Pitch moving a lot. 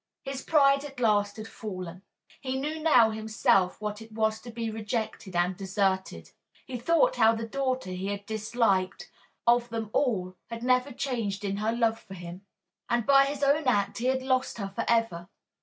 No: average, 4.2 semitones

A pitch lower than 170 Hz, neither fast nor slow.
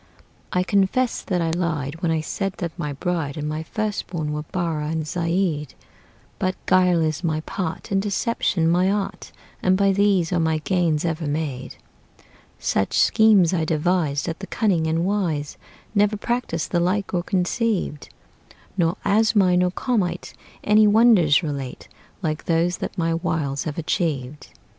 No: medium, 175 Hz; average, 155 wpm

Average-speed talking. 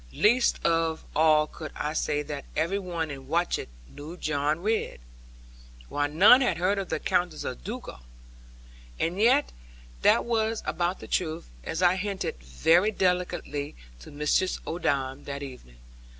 Yes: average, 150 wpm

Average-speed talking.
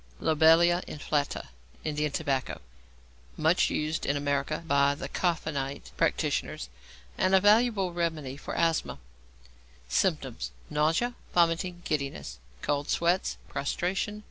No: slow, 105 wpm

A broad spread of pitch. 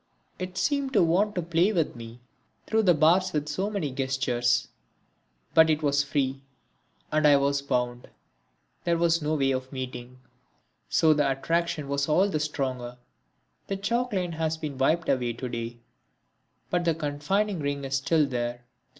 No: average, 4.4 semitones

